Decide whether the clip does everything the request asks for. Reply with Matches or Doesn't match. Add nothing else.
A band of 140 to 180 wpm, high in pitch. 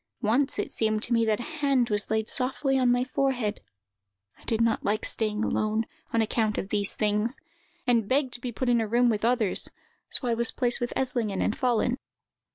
Doesn't match